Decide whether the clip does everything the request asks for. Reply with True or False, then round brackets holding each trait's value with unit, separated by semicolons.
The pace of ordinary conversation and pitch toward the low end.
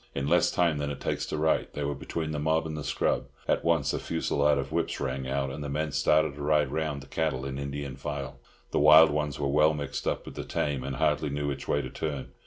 False (255 wpm; 75 Hz)